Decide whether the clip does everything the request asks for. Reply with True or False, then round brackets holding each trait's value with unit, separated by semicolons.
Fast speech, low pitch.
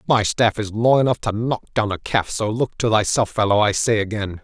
True (245 wpm; 110 Hz)